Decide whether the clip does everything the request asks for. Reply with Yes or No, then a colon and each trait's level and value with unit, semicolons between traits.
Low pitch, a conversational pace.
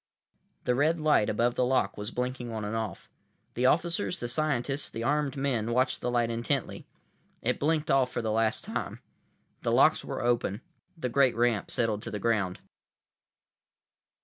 Yes: low, 120 Hz; average, 175 wpm